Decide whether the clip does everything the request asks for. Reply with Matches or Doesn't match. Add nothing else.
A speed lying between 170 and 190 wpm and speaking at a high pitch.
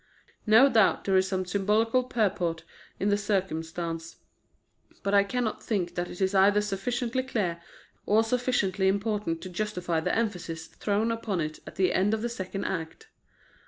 Doesn't match